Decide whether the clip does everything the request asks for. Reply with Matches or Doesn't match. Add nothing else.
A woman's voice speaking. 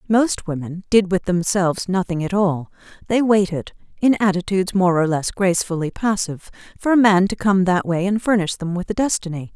Matches